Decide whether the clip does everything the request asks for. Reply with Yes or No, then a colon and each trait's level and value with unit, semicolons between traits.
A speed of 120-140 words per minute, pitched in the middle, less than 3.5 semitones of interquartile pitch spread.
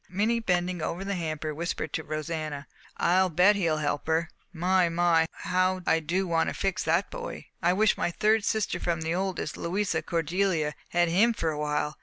No: average, 190 wpm; medium, 175 Hz; average, 2.8 semitones